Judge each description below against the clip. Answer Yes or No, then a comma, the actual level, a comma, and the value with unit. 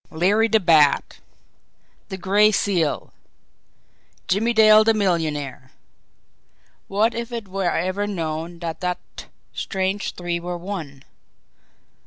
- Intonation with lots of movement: No, average, 3.7 semitones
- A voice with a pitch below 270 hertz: Yes, medium, 185 Hz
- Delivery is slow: Yes, slow, 110 wpm